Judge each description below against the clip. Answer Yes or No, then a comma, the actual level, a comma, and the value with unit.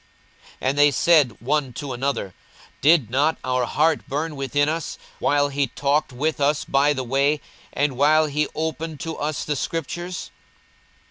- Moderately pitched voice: Yes, medium, 145 Hz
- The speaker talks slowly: No, average, 160 wpm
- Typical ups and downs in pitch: No, narrow, 2.1 semitones